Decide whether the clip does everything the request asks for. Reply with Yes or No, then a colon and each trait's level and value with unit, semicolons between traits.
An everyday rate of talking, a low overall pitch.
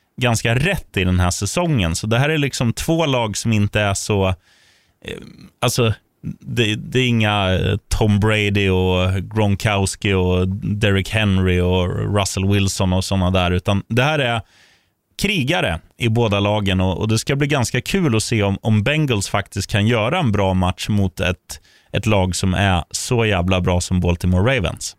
Yes: average, 175 wpm; low, 100 Hz